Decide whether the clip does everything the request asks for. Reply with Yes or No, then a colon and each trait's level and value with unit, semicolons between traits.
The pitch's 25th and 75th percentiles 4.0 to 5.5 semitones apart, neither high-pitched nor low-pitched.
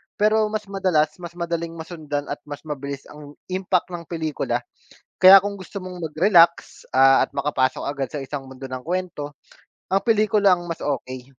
Yes: average, 4.4 semitones; medium, 165 Hz